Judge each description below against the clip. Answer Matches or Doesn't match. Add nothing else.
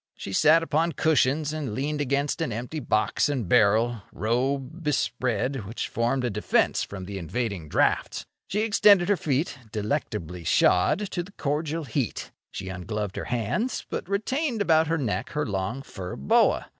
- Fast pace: Doesn't match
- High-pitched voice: Doesn't match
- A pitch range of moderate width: Doesn't match